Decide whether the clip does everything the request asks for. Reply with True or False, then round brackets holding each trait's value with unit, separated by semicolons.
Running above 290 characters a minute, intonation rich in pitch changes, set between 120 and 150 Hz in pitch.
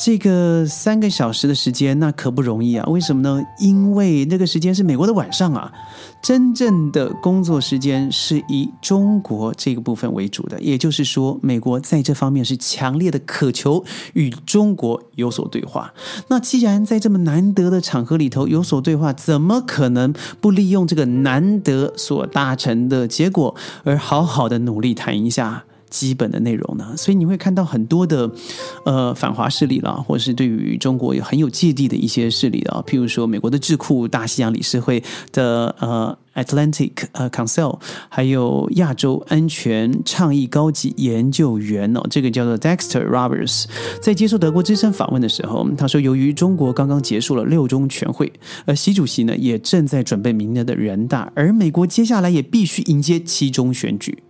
True (305 characters per minute; 5.8 semitones; 140 Hz)